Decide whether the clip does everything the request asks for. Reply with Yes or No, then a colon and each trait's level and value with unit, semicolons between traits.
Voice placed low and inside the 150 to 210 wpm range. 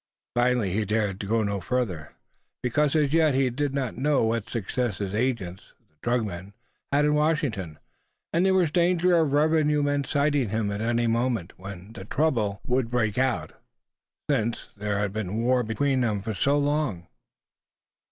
Yes: low, 120 Hz; average, 165 wpm